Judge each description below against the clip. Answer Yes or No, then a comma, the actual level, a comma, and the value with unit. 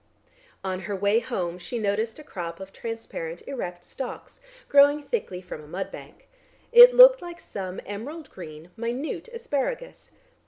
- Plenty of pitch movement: Yes, wide, 8.2 semitones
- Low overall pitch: No, high, 225 Hz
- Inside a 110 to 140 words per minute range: No, average, 150 wpm